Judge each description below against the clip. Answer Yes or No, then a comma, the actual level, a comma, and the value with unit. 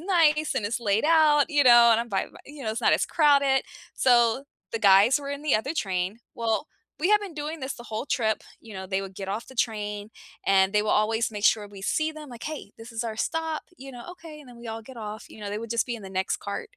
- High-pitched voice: Yes, high, 235 Hz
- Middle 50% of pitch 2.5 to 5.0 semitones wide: No, wide, 5.5 semitones